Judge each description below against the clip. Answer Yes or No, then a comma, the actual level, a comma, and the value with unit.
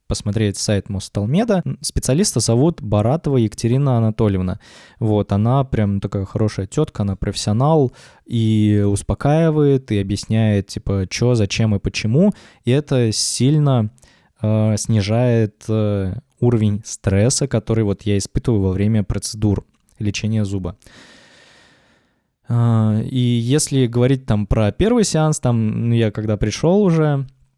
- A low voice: Yes, low, 110 Hz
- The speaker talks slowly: No, average, 120 wpm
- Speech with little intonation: No, average, 4.0 semitones